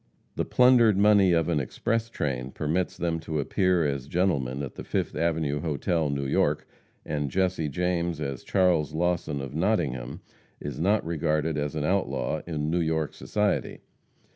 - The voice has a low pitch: Yes, very low, 80 Hz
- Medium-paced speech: Yes, average, 160 wpm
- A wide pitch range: No, average, 3.8 semitones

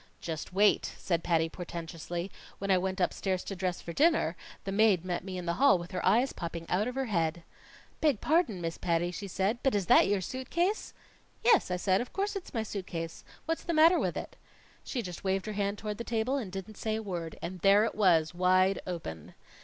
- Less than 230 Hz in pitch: Yes, high, 190 Hz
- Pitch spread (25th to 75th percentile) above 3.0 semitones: Yes, average, 4.1 semitones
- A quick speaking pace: Yes, fast, 225 wpm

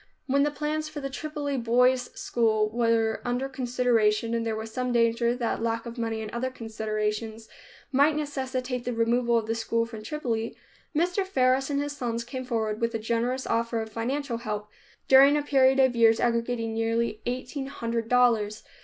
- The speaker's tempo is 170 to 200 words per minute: Yes, average, 180 wpm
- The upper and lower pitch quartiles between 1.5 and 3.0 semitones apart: Yes, narrow, 2.5 semitones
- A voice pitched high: Yes, high, 235 Hz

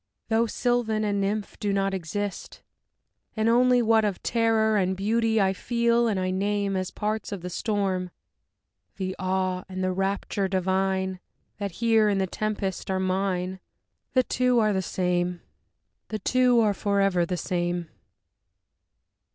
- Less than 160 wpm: Yes, average, 150 wpm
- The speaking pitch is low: No, high, 200 Hz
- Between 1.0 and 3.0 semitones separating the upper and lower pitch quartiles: Yes, average, 2.7 semitones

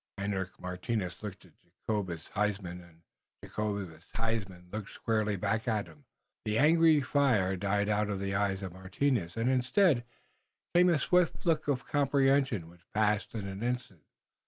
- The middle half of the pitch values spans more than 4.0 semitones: Yes, average, 4.9 semitones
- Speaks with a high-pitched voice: No, low, 105 Hz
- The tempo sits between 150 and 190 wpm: Yes, average, 155 wpm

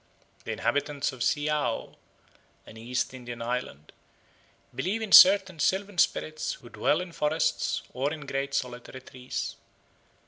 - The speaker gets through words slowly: Yes, slow, 130 wpm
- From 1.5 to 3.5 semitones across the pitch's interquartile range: No, average, 4.2 semitones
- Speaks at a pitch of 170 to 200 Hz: No, medium, 140 Hz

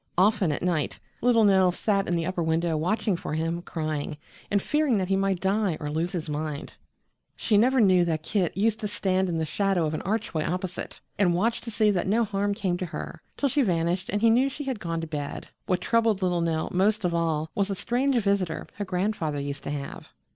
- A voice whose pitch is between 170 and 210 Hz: Yes, medium, 185 Hz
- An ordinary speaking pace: No, fast, 225 wpm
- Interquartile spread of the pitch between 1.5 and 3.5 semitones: No, average, 4.0 semitones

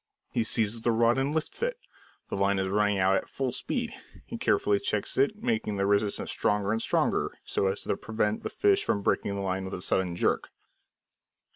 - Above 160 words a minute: Yes, average, 200 wpm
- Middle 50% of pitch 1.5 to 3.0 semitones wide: No, average, 3.5 semitones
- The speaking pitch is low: Yes, low, 105 Hz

